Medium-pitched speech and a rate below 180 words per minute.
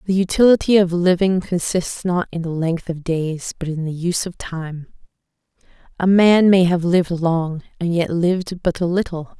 No: medium, 175 Hz; average, 185 wpm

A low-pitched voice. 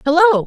No: very high, 320 Hz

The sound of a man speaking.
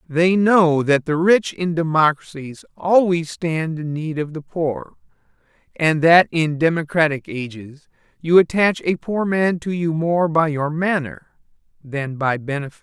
Yes: male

